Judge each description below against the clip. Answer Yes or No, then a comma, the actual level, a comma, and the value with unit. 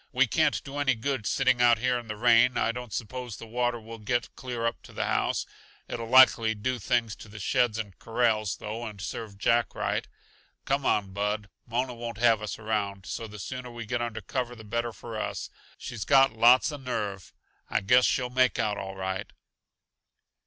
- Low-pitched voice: Yes, low, 115 Hz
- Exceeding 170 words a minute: Yes, average, 200 wpm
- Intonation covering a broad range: No, narrow, 2.5 semitones